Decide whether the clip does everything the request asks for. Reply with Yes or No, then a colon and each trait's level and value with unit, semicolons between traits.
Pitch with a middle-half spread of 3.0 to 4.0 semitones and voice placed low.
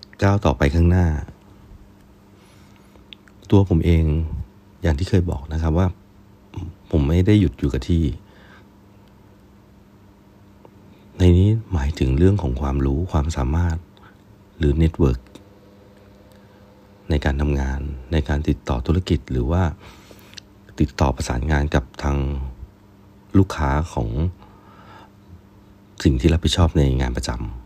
No: average, 4.4 semitones; very low, 95 Hz